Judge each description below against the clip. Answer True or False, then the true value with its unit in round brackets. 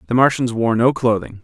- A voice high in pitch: False (115 Hz)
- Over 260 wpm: False (210 wpm)